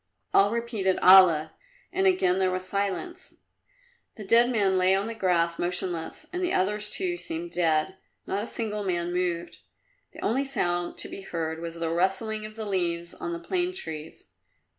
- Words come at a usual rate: Yes, average, 175 wpm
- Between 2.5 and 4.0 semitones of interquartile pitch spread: No, average, 4.7 semitones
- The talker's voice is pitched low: No, high, 190 Hz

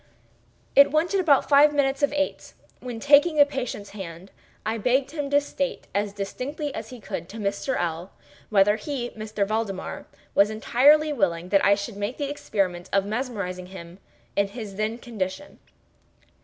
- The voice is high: Yes, high, 220 Hz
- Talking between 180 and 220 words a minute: No, average, 165 wpm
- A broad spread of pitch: Yes, wide, 6.1 semitones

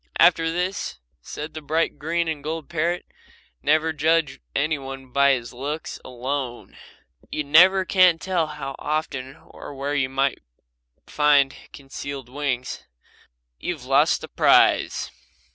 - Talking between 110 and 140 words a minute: Yes, slow, 135 wpm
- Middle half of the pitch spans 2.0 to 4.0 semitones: Yes, average, 3.0 semitones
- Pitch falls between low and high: Yes, medium, 150 Hz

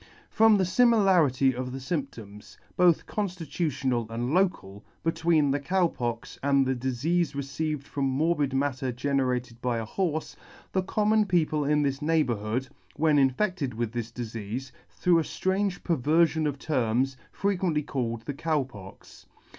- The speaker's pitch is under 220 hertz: Yes, medium, 140 Hz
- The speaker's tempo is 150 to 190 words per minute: No, average, 140 wpm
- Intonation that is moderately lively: Yes, average, 4.9 semitones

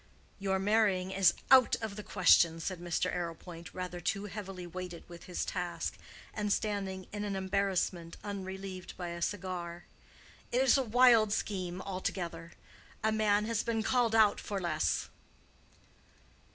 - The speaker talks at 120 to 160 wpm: Yes, average, 145 wpm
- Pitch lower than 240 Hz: Yes, high, 190 Hz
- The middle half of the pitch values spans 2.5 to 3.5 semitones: Yes, average, 2.9 semitones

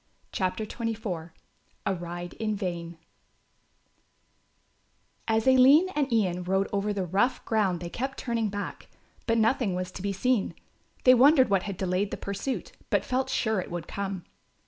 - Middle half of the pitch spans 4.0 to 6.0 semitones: Yes, average, 4.4 semitones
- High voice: Yes, high, 205 Hz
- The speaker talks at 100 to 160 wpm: Yes, average, 155 wpm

